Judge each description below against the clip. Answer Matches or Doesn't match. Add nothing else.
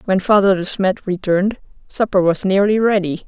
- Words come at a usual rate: Matches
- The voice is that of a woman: Matches